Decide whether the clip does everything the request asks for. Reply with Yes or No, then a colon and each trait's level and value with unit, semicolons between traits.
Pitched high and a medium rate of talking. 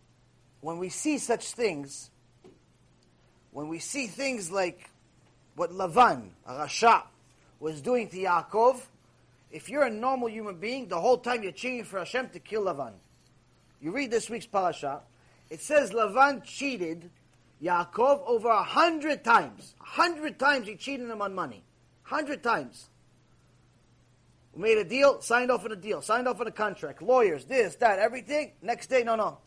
Yes: high, 230 Hz; average, 165 wpm